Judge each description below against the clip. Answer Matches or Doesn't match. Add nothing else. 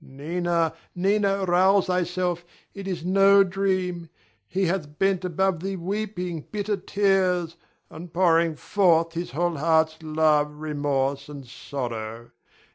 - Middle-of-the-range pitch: Matches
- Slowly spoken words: Matches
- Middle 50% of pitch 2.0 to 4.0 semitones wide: Matches